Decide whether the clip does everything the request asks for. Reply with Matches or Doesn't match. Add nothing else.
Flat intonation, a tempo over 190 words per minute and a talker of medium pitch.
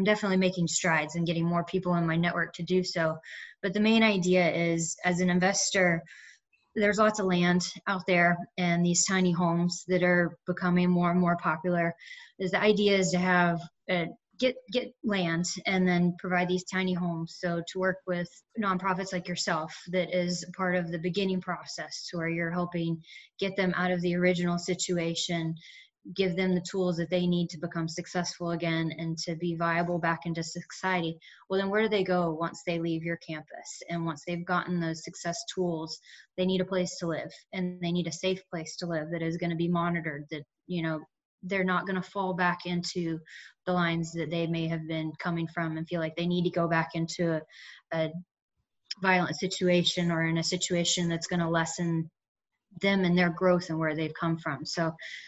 Matches